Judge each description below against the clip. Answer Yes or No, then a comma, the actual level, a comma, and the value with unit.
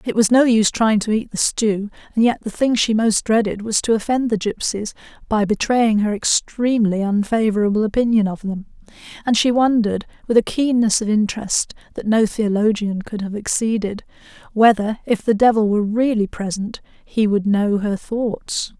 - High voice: Yes, high, 215 Hz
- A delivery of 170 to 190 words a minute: Yes, average, 175 wpm